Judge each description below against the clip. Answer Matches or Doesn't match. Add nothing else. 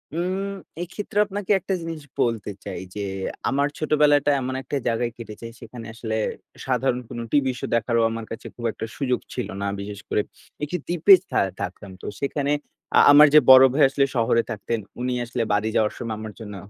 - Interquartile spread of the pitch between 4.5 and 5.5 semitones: Matches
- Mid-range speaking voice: Doesn't match